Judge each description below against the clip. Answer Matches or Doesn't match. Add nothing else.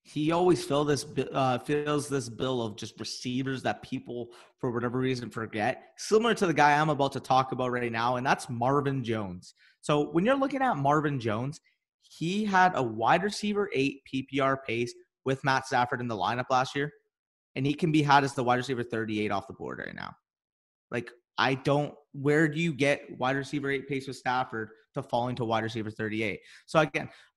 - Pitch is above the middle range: Doesn't match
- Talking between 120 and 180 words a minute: Doesn't match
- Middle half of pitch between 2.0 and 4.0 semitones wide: Matches